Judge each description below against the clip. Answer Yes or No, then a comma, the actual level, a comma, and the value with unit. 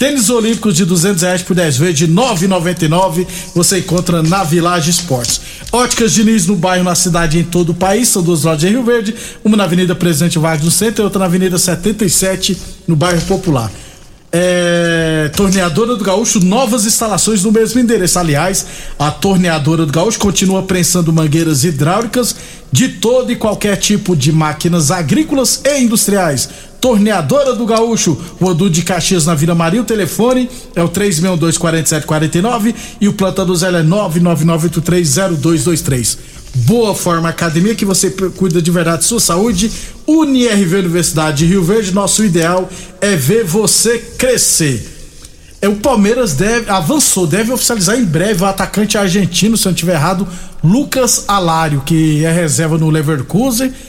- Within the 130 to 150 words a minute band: No, average, 160 wpm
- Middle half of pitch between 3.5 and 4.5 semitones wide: Yes, average, 4.2 semitones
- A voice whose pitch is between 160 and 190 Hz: Yes, medium, 185 Hz